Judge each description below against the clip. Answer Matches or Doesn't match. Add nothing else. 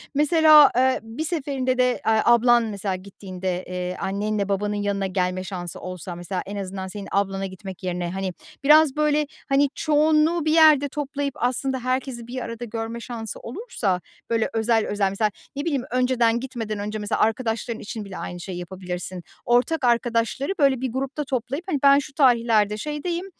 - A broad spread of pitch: Matches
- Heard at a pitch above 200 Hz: Matches